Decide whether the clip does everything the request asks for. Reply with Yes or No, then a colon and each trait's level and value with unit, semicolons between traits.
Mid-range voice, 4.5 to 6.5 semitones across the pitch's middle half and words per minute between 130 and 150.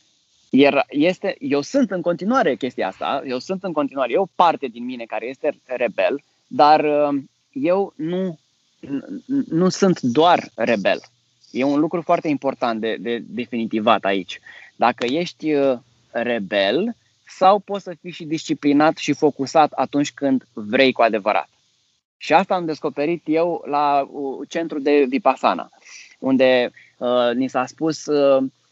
Yes: medium, 145 Hz; average, 4.8 semitones; average, 140 wpm